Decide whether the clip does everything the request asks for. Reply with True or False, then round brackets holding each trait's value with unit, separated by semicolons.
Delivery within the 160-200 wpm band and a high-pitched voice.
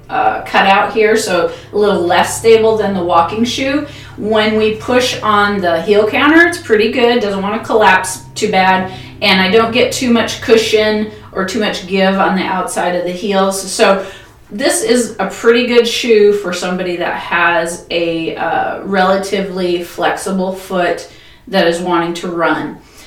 True (175 wpm; 195 Hz)